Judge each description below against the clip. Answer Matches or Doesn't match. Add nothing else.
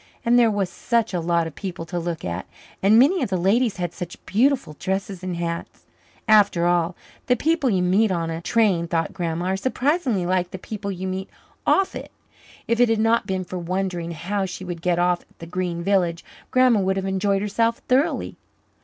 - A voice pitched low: Doesn't match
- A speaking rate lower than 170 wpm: Doesn't match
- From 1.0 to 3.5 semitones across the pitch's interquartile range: Doesn't match